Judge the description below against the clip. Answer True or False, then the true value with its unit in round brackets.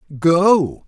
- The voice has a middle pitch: True (165 Hz)